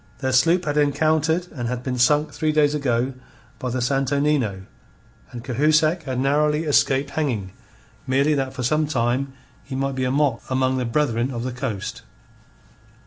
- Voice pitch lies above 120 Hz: Yes, low, 135 Hz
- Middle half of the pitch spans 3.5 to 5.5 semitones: No, average, 3.0 semitones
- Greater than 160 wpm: Yes, average, 170 wpm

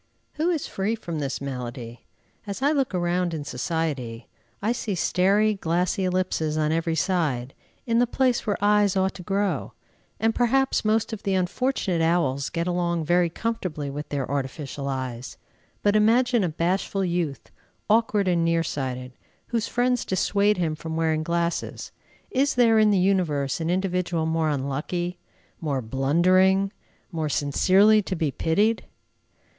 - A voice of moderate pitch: Yes, medium, 175 Hz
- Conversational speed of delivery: Yes, average, 150 wpm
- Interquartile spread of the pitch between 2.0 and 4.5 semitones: No, average, 5.1 semitones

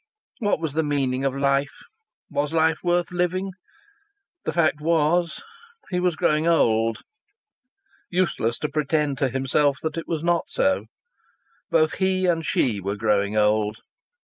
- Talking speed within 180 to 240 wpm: No, average, 145 wpm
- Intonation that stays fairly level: No, average, 4.6 semitones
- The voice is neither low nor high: Yes, medium, 150 Hz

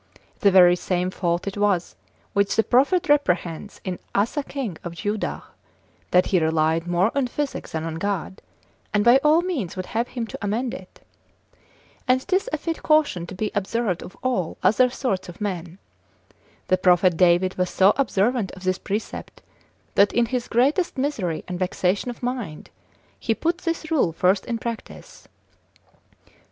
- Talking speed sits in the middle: Yes, average, 165 wpm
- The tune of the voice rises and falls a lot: Yes, wide, 5.7 semitones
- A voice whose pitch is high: Yes, high, 200 Hz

